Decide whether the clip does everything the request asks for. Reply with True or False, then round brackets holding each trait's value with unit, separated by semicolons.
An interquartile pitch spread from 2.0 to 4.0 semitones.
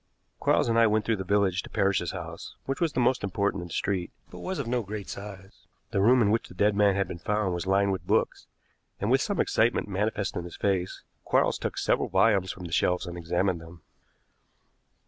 True (2.9 semitones)